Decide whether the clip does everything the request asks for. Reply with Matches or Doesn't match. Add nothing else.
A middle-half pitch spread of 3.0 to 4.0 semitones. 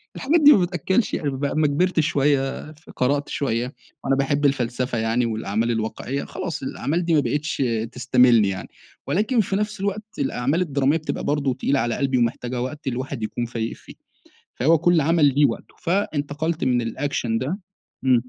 Doesn't match